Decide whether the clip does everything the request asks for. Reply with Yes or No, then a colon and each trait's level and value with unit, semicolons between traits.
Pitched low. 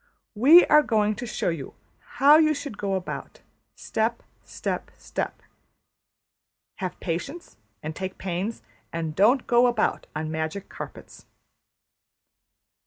No: high, 210 Hz